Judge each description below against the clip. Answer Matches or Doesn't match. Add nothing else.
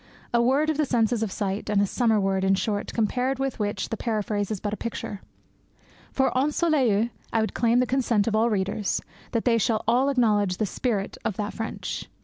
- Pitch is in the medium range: Doesn't match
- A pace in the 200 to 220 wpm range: Matches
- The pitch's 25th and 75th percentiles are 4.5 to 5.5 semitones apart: Doesn't match